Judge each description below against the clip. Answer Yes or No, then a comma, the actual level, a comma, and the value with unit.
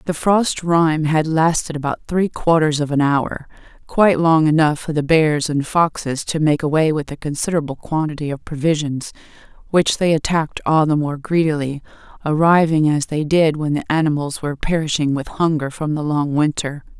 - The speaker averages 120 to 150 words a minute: No, average, 175 wpm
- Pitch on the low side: No, medium, 155 Hz